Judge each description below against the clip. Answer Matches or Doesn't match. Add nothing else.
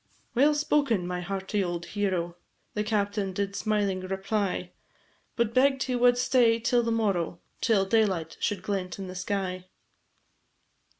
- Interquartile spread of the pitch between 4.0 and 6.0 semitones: Doesn't match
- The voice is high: Matches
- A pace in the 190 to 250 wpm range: Doesn't match